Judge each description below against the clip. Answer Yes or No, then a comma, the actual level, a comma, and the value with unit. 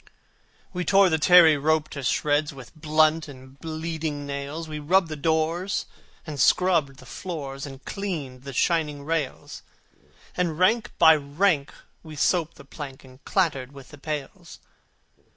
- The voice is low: No, medium, 155 Hz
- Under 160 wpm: Yes, average, 150 wpm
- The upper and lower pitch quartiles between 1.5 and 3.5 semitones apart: Yes, average, 2.9 semitones